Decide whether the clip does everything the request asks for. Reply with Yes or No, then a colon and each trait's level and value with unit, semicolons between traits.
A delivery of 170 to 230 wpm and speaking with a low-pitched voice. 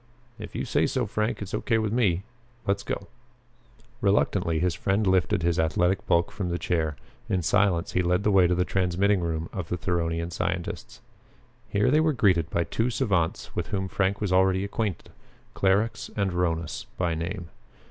Yes: average, 180 wpm; very low, 95 Hz